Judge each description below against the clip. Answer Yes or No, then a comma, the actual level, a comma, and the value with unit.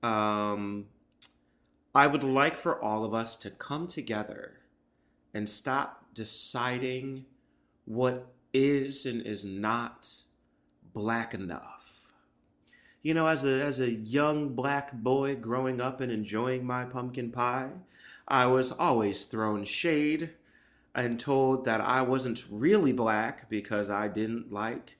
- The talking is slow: Yes, slow, 125 wpm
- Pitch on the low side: Yes, low, 120 Hz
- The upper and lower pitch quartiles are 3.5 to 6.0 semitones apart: Yes, average, 4.1 semitones